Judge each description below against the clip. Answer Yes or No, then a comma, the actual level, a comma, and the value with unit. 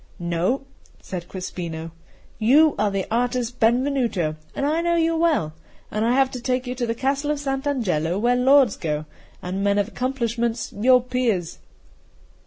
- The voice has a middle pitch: No, high, 240 Hz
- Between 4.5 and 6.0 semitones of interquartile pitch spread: Yes, wide, 5.6 semitones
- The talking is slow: No, average, 165 wpm